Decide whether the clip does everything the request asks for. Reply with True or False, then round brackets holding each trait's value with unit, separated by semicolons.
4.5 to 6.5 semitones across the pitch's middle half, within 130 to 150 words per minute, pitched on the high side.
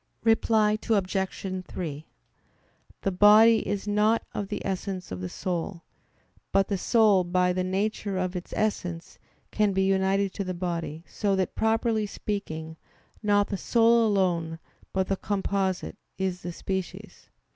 False (2.5 semitones; 145 wpm; 195 Hz)